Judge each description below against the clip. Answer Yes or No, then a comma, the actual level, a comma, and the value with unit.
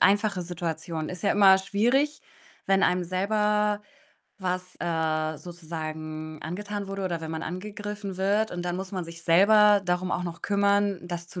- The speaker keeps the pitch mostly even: No, average, 3.2 semitones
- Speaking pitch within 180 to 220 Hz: Yes, medium, 185 Hz